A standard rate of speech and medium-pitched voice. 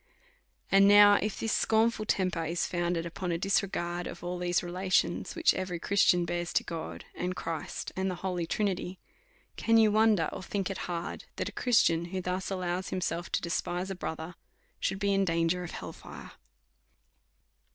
Yes: average, 180 wpm; medium, 180 Hz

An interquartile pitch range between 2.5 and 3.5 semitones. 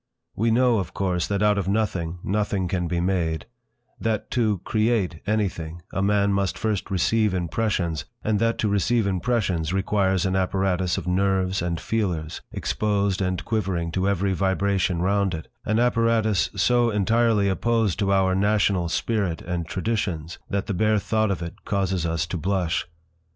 Yes: average, 3.0 semitones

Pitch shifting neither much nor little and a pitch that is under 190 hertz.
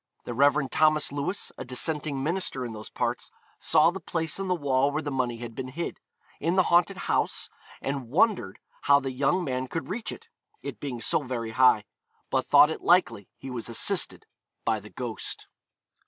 Yes: average, 4.5 semitones; medium, 140 Hz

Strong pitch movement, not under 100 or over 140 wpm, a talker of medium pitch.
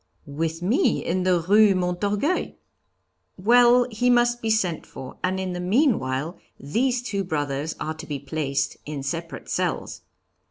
No: wide, 6.5 semitones; average, 150 wpm; medium, 180 Hz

